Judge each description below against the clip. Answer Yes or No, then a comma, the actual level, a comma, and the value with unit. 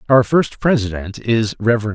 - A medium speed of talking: Yes, average, 155 wpm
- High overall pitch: No, low, 115 Hz